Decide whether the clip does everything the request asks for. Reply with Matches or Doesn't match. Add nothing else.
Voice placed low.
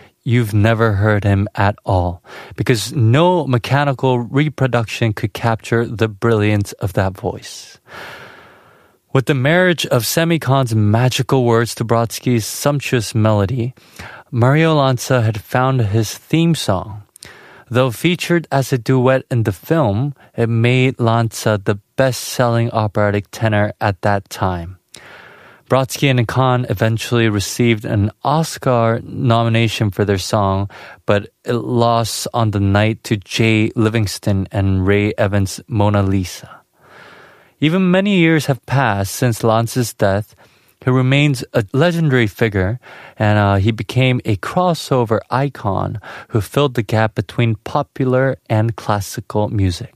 Matches